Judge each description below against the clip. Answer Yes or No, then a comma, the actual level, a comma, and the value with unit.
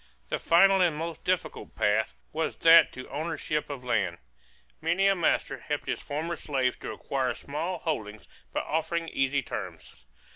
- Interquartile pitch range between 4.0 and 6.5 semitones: Yes, average, 4.3 semitones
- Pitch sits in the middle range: Yes, medium, 150 Hz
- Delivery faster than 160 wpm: No, average, 155 wpm